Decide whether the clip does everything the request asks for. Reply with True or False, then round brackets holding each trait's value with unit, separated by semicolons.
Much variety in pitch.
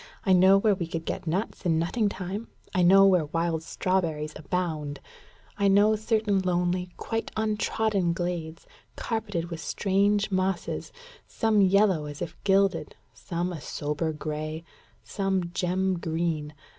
False (3.2 semitones)